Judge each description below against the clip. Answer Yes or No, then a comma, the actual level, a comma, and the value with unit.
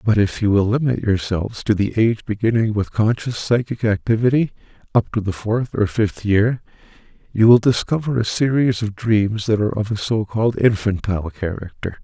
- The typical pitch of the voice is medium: No, low, 110 Hz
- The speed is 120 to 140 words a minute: No, average, 175 wpm